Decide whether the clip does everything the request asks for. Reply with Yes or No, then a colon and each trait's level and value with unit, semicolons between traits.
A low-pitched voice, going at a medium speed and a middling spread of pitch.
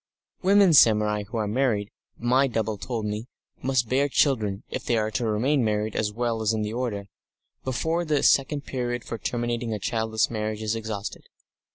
Yes: low, 115 Hz; average, 180 wpm; average, 3.2 semitones